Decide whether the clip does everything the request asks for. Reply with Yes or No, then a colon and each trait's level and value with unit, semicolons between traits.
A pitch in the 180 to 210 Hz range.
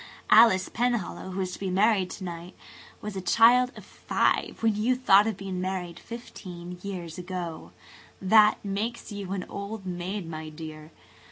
Yes: high, 190 Hz